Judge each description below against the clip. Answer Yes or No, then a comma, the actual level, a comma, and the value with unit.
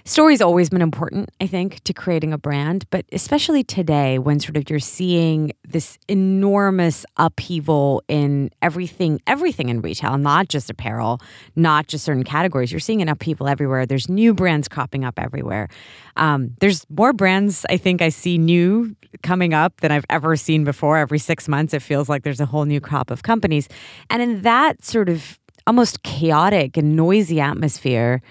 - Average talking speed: Yes, average, 175 wpm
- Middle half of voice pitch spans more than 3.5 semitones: Yes, average, 4.5 semitones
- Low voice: No, medium, 160 Hz